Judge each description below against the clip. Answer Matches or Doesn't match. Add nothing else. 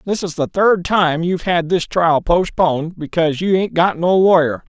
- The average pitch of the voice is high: Doesn't match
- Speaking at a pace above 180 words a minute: Matches